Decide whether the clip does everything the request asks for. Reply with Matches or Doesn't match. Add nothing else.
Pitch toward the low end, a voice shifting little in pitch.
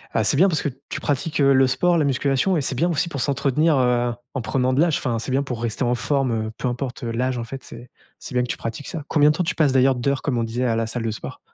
Doesn't match